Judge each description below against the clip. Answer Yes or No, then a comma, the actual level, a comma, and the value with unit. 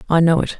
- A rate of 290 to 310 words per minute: Yes, fast, 300 wpm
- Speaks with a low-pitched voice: No, medium, 165 Hz